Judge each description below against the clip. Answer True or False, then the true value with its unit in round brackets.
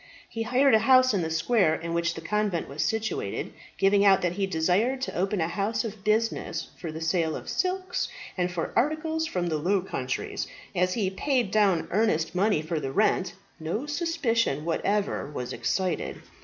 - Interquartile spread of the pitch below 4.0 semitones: False (5.4 semitones)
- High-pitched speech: True (195 Hz)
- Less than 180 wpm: False (185 wpm)